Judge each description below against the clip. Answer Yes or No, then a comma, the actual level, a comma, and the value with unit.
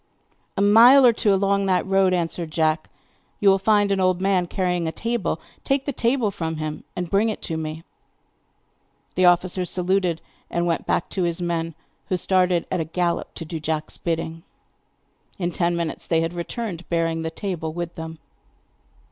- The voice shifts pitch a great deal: No, average, 3.0 semitones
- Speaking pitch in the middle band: Yes, medium, 175 Hz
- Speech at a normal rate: Yes, average, 180 wpm